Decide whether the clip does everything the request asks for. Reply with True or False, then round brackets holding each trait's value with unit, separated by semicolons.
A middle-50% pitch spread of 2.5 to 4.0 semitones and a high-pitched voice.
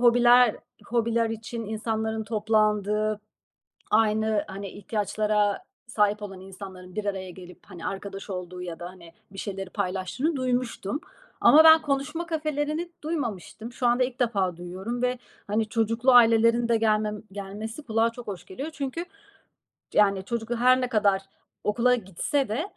True (3.6 semitones; 220 Hz)